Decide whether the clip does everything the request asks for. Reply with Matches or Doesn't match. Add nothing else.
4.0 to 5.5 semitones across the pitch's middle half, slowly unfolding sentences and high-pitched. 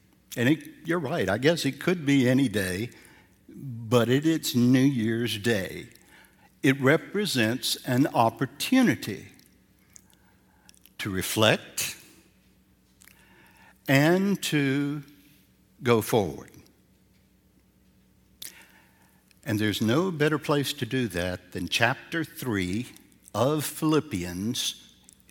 Doesn't match